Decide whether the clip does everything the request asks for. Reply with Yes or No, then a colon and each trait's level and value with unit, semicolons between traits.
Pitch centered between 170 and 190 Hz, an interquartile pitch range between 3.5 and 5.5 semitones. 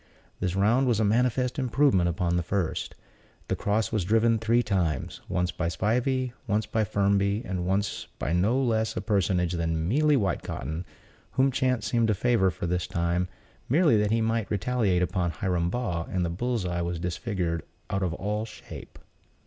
No: low, 100 Hz; average, 4.7 semitones